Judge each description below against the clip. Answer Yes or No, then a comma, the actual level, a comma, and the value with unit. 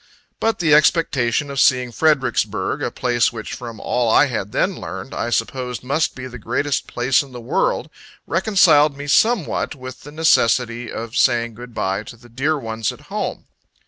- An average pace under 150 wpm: No, average, 175 wpm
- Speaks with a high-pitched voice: No, low, 125 Hz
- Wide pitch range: No, average, 3.6 semitones